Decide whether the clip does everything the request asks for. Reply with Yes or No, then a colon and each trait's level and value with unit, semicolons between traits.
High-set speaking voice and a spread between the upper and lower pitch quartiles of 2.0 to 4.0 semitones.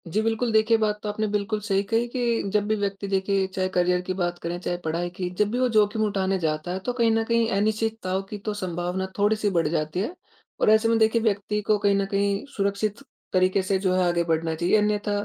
Yes: high, 200 Hz; average, 2.8 semitones